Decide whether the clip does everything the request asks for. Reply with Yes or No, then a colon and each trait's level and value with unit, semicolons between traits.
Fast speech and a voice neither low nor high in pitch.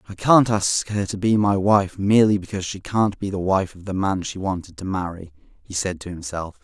No: fast, 235 wpm; very low, 95 Hz